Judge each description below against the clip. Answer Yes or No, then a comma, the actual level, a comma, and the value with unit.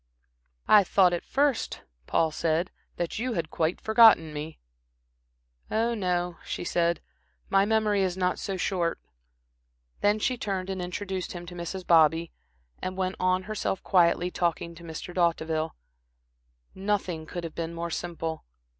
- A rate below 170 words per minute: Yes, average, 145 wpm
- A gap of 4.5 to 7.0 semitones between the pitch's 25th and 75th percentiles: No, narrow, 2.6 semitones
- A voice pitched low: No, medium, 180 Hz